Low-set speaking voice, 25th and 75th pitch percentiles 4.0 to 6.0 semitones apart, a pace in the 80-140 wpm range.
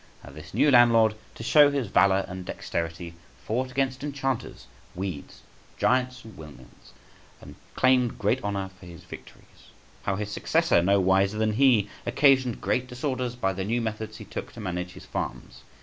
No: low, 110 Hz; average, 5.1 semitones; average, 165 wpm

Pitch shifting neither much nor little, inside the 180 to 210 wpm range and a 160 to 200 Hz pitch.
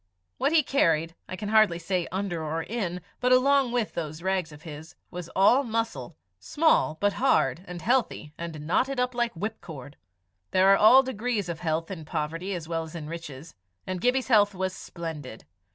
No: wide, 5.9 semitones; average, 185 wpm; medium, 185 Hz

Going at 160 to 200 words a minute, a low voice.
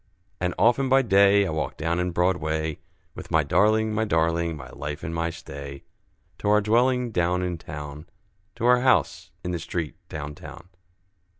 Yes: average, 175 wpm; very low, 90 Hz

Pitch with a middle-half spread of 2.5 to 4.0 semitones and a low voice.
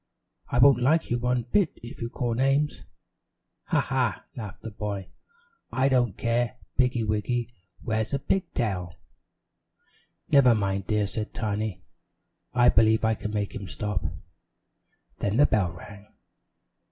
Yes: average, 3.2 semitones; low, 115 Hz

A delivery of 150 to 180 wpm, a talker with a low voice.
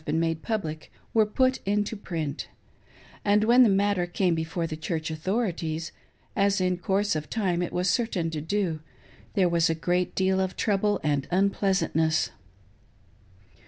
No: average, 160 wpm; medium, 180 Hz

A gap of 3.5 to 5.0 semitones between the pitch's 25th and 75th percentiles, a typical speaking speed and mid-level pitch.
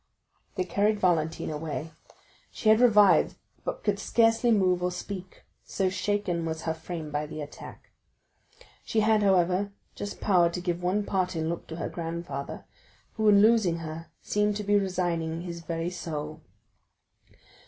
Yes: average, 3.8 semitones; average, 155 wpm; medium, 180 Hz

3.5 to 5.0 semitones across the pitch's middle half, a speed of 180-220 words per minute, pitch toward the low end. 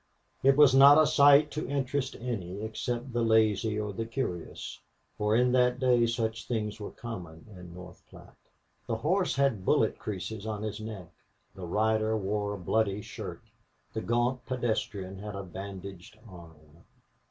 No: average, 4.0 semitones; average, 160 wpm; low, 110 Hz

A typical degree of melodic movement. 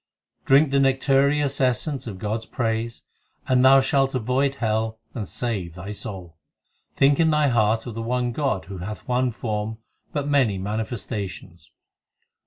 Yes: average, 4.1 semitones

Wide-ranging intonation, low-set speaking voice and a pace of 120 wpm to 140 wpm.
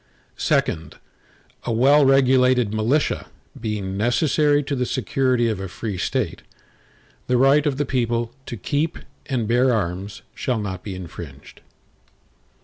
No: average, 4.5 semitones; low, 120 Hz; slow, 135 wpm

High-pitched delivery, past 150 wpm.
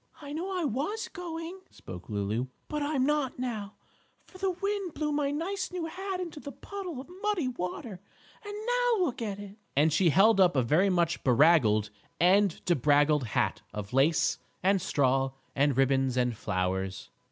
Yes: high, 200 Hz; average, 170 wpm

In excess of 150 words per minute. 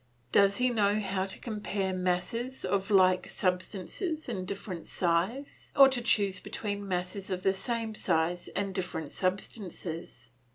No: average, 140 wpm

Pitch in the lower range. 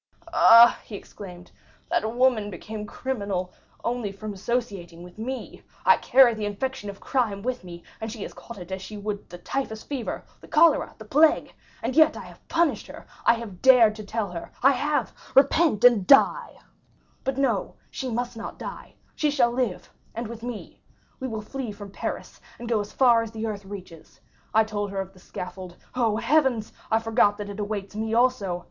No: high, 220 Hz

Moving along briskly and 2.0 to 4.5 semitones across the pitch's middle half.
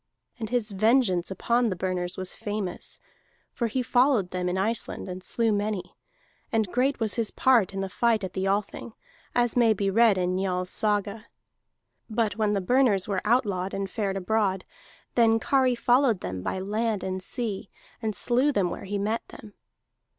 No: average, 175 wpm; average, 3.6 semitones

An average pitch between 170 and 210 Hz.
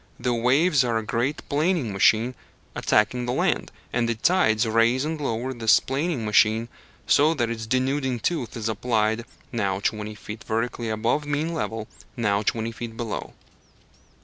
No: low, 115 Hz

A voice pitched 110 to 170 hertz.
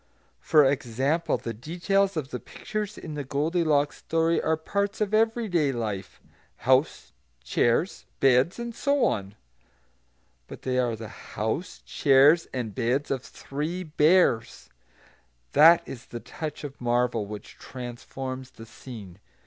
Yes: medium, 140 Hz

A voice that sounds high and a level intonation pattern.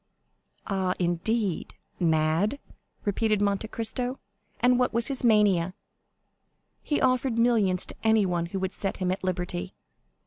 No: high, 200 Hz; average, 4.1 semitones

